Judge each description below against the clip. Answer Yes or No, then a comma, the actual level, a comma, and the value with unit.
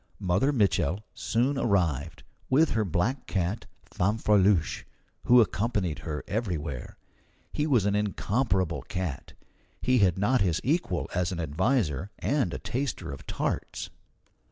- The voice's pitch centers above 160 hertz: No, low, 100 Hz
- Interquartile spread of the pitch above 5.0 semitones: Yes, wide, 5.5 semitones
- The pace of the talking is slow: Yes, slow, 130 wpm